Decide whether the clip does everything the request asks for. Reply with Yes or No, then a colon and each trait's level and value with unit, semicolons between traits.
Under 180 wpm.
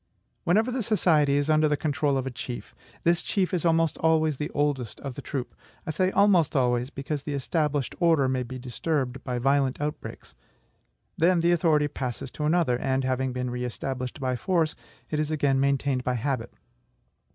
No: average, 185 wpm